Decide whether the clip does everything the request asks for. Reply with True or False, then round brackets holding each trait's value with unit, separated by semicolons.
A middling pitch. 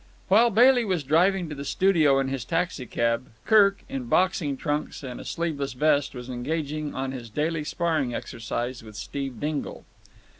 True (145 Hz)